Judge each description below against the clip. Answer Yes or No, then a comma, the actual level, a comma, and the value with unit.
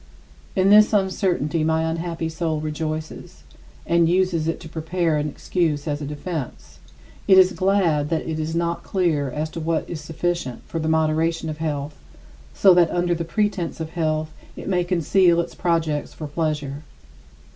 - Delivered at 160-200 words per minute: Yes, average, 165 wpm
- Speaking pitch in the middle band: Yes, medium, 165 Hz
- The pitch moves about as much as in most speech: No, narrow, 2.1 semitones